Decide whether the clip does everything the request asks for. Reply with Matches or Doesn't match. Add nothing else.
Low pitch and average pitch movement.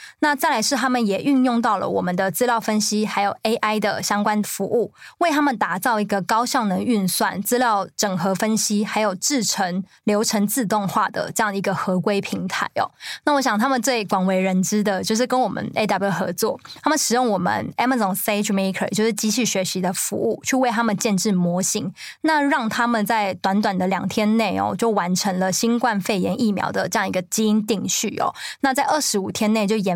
Doesn't match